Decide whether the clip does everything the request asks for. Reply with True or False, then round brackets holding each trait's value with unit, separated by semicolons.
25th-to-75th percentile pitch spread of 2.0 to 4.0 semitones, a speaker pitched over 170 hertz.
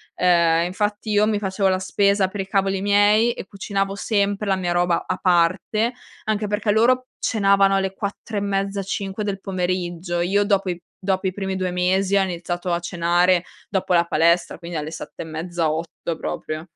True (2.5 semitones; 190 Hz)